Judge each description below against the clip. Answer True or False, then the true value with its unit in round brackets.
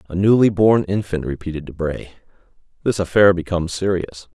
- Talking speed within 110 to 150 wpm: True (135 wpm)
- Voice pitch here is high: False (90 Hz)